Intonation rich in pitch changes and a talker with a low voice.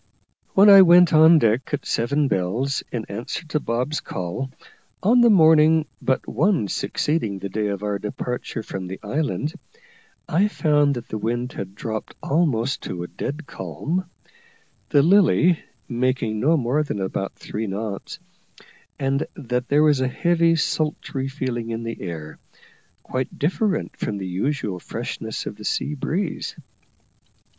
Yes: wide, 6.3 semitones; low, 130 Hz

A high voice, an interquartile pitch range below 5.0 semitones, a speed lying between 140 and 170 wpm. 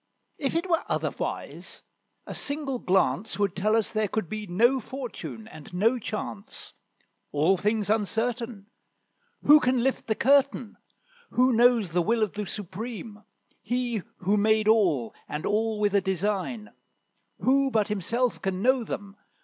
Yes: high, 220 Hz; average, 3.3 semitones; average, 150 wpm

